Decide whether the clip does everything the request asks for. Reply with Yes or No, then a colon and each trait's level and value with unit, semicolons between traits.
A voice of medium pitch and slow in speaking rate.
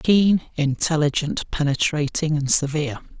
Yes: medium, 150 Hz; slow, 95 wpm